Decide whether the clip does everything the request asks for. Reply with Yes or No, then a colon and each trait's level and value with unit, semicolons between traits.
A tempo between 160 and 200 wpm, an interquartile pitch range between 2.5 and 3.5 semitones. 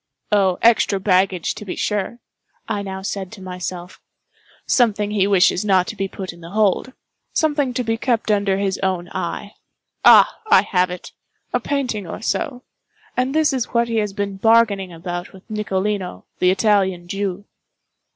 No: average, 150 wpm; average, 3.2 semitones